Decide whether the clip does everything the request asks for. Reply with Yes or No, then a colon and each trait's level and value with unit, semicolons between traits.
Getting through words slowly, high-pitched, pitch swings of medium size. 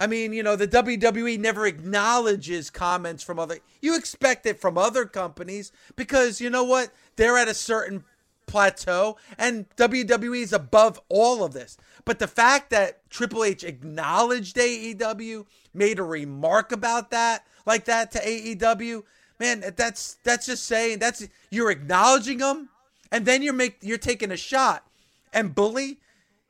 No: average, 155 wpm; high, 225 Hz; average, 3.0 semitones